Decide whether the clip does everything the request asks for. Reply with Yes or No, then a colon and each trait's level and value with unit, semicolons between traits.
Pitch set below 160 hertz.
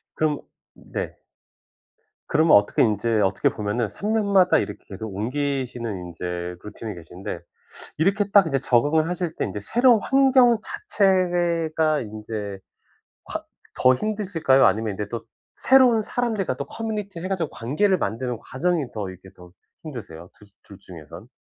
Yes: medium, 140 Hz